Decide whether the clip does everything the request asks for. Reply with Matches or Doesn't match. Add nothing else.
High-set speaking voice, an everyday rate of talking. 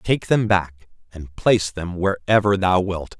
Doesn't match